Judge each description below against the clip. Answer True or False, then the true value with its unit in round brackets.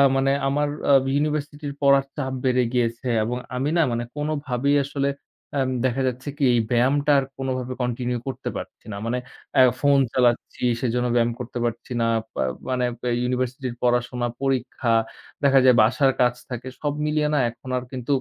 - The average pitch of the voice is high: False (130 Hz)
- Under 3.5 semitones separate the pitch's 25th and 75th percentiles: True (2.4 semitones)